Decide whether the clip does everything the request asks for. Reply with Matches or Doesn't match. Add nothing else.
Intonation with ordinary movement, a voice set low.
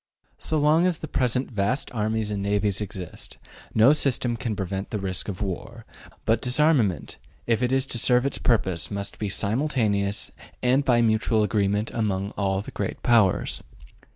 Matches